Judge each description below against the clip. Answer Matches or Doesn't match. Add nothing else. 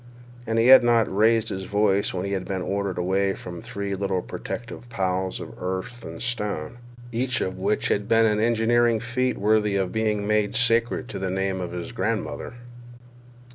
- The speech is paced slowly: Doesn't match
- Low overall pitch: Matches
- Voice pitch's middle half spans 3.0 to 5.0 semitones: Matches